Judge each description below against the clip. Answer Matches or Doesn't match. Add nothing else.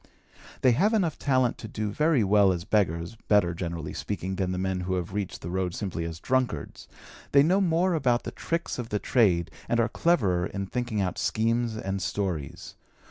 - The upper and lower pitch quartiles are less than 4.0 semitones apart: Doesn't match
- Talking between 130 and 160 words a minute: Doesn't match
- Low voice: Matches